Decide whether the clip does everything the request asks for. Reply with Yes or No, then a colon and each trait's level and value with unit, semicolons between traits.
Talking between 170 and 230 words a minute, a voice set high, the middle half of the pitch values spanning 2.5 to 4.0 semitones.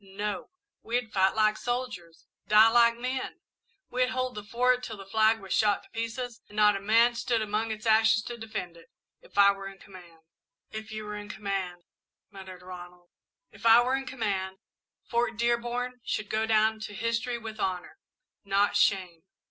Yes: average, 180 wpm; high, 215 Hz; average, 3.2 semitones